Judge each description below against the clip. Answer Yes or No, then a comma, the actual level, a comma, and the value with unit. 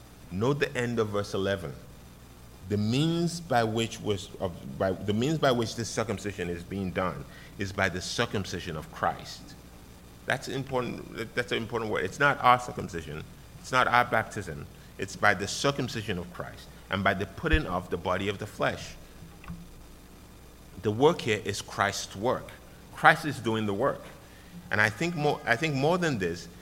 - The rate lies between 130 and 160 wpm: No, average, 175 wpm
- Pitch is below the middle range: Yes, low, 105 Hz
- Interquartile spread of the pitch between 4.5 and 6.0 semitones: Yes, wide, 5.4 semitones